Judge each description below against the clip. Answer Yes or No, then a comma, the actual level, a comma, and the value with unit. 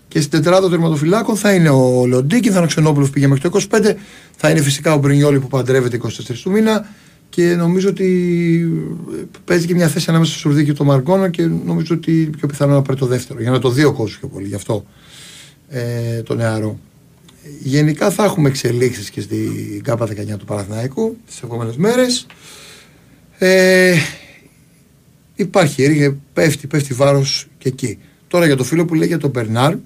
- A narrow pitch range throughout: No, average, 4.8 semitones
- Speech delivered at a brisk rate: Yes, fast, 180 wpm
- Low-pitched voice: No, medium, 150 Hz